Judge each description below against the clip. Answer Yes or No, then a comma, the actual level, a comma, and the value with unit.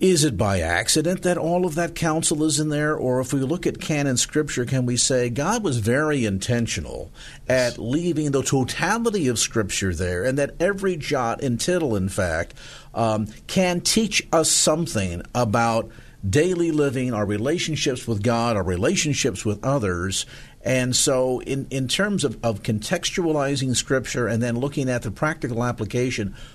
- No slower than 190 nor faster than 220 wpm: No, average, 165 wpm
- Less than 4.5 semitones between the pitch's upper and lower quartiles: No, average, 5.2 semitones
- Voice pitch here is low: Yes, low, 130 Hz